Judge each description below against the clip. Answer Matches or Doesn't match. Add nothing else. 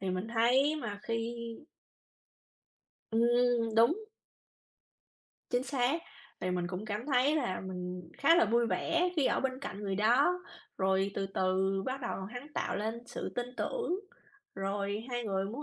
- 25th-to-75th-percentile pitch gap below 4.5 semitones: Doesn't match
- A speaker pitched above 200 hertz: Matches